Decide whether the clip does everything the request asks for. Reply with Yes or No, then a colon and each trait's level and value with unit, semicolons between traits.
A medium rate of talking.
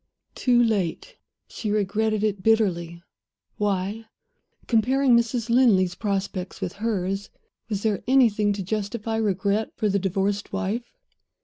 No: slow, 120 wpm